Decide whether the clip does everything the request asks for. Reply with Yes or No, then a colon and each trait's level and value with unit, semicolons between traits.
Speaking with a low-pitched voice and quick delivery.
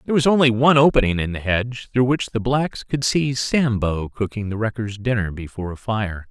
Yes: low, 115 Hz; fast, 210 wpm